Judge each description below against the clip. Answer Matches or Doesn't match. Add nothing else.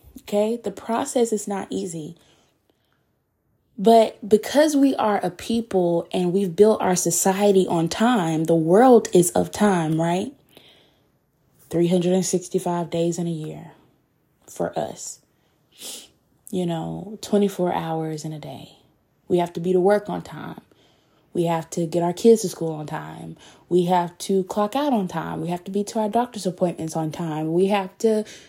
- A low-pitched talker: Doesn't match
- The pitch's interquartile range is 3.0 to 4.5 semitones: Matches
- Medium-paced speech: Matches